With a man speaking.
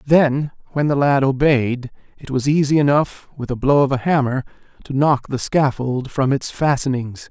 Yes: male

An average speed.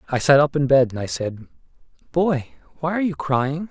No: fast, 210 wpm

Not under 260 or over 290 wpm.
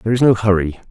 Yes: fast, 265 wpm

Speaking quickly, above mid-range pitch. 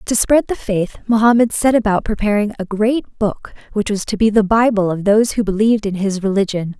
Yes: fast, 210 wpm; high, 210 Hz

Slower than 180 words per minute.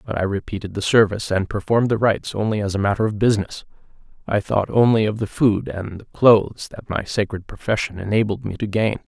No: fast, 205 wpm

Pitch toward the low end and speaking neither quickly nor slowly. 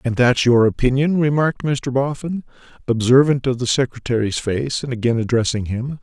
Yes: low, 130 Hz; average, 160 wpm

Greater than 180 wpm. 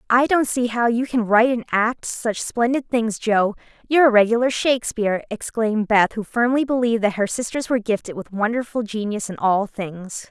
Yes: average, 190 wpm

